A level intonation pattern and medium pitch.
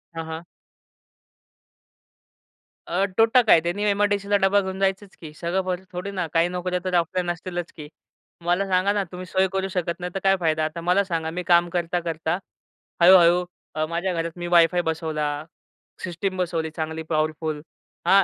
Yes: narrow, 2.3 semitones; medium, 175 Hz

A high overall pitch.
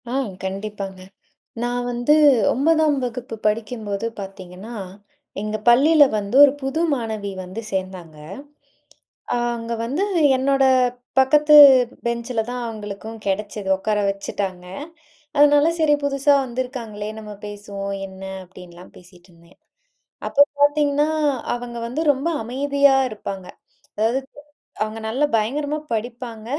Yes: high, 230 Hz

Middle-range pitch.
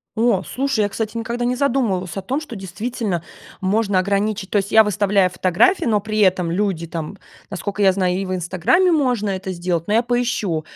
No: high, 205 Hz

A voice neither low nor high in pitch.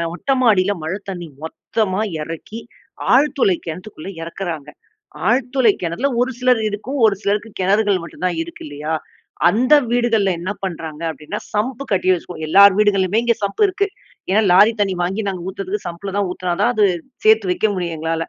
No: high, 195 Hz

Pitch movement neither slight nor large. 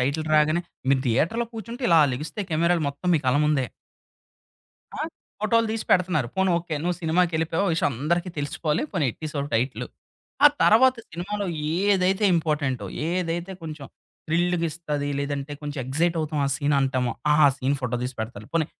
Yes: average, 3.9 semitones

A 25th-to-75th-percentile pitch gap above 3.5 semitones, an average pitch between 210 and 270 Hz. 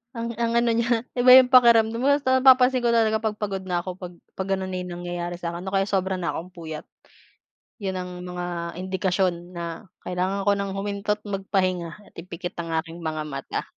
No: average, 4.0 semitones; high, 190 Hz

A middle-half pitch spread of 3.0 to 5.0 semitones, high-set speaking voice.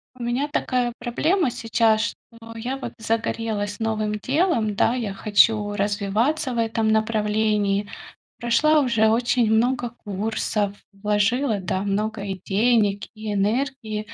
No: narrow, 2.6 semitones; high, 220 Hz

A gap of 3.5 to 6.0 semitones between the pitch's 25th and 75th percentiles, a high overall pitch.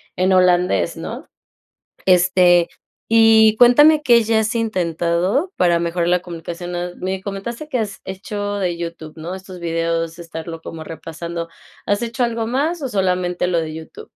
No: average, 4.6 semitones; medium, 180 Hz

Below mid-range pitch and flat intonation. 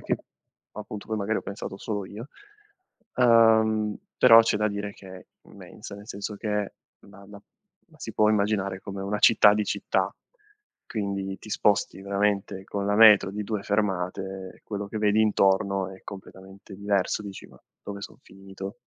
Yes: low, 100 Hz; narrow, 1.5 semitones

